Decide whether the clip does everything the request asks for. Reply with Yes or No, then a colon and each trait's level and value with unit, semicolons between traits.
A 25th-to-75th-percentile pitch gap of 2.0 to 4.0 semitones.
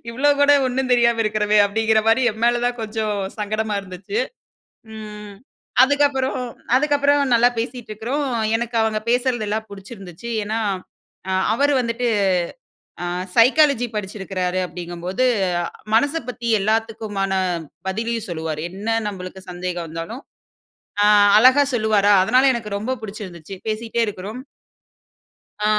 Yes: average, 3.5 semitones